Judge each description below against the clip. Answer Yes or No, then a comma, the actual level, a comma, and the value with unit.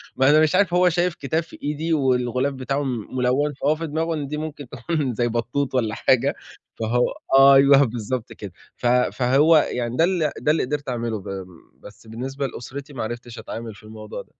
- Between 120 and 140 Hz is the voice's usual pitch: Yes, low, 135 Hz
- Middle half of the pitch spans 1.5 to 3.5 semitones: No, average, 4.0 semitones